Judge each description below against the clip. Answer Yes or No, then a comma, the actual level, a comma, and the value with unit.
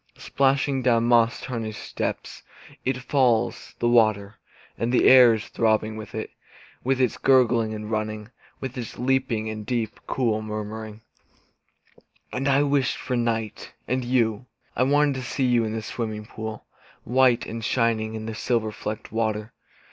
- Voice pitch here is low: Yes, low, 115 Hz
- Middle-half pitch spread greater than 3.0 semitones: No, average, 2.7 semitones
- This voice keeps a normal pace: Yes, average, 155 wpm